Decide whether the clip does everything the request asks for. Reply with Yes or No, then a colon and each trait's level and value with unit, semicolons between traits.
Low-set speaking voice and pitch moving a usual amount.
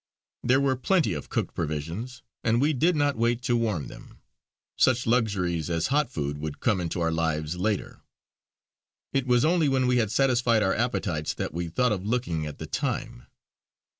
No: low, 110 Hz; wide, 7.2 semitones